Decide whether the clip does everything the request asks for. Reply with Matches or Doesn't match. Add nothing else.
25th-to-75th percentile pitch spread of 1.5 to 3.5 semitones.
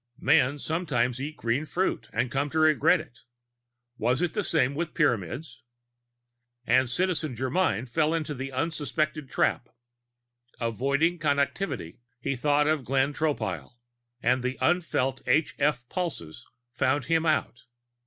Doesn't match